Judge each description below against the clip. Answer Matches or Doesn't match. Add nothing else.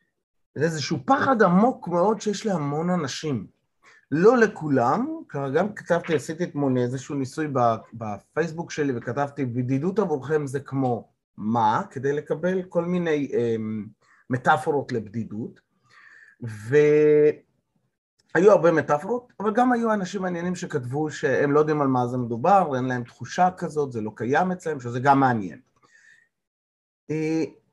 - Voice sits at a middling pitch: Matches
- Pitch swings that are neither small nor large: Doesn't match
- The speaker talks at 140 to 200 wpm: Doesn't match